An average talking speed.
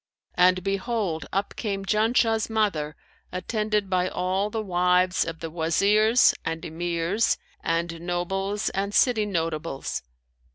No: slow, 120 wpm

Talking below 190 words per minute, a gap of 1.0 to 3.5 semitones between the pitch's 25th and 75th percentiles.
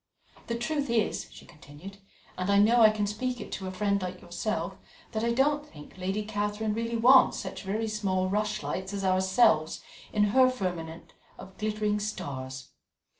Yes: average, 170 wpm; average, 3.2 semitones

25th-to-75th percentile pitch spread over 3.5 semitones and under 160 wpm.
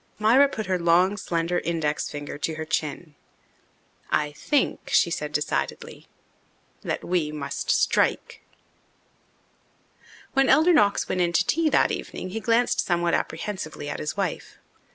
Yes: average, 5.3 semitones; average, 140 wpm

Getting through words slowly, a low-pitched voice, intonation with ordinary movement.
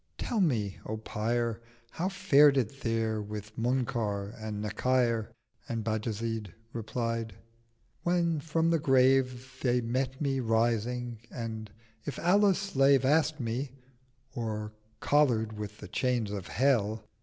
Yes: slow, 125 wpm; low, 120 Hz; average, 3.6 semitones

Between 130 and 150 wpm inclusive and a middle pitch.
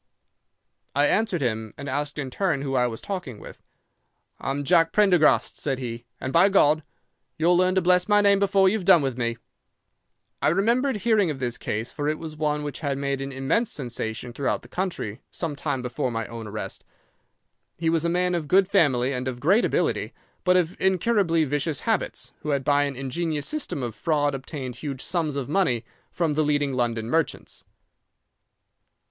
No: average, 185 wpm; medium, 150 Hz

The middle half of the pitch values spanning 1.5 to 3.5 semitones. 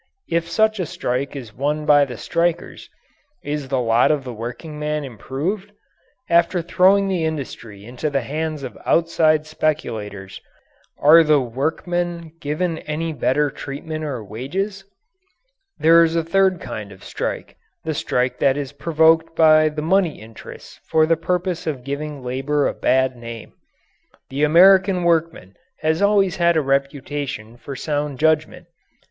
No: average, 3.9 semitones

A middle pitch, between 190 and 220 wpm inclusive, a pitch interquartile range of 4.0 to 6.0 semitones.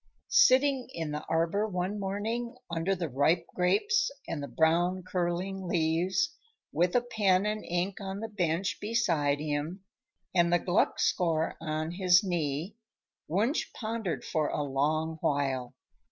No: medium, 180 Hz; average, 140 wpm; average, 4.3 semitones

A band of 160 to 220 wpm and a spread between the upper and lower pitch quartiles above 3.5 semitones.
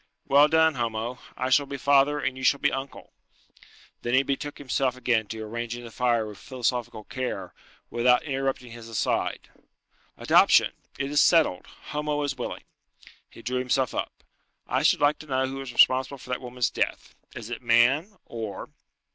No: average, 170 wpm; average, 2.7 semitones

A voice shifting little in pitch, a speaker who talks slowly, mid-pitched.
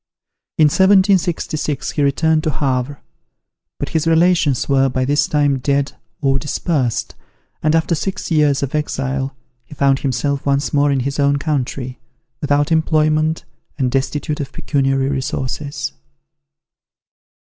Yes: narrow, 2.3 semitones; slow, 130 wpm; medium, 145 Hz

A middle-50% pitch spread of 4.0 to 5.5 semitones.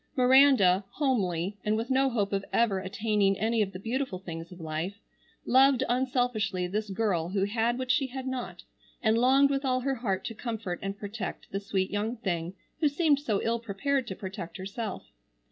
Yes: average, 4.7 semitones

